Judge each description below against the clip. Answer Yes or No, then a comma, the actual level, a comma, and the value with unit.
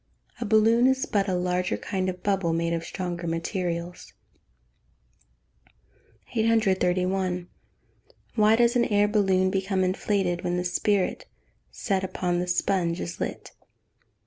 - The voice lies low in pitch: No, medium, 185 Hz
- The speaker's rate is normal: No, slow, 125 wpm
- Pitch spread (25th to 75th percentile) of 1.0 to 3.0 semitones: Yes, narrow, 2.6 semitones